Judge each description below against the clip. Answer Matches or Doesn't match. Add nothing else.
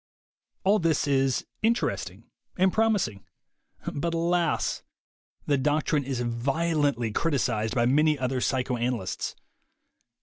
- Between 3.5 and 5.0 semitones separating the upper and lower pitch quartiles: Doesn't match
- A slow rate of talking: Matches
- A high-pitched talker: Doesn't match